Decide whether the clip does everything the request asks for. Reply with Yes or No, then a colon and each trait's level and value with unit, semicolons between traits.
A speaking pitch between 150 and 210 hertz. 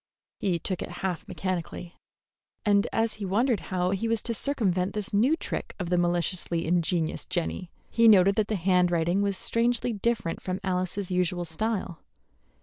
Yes: medium, 185 Hz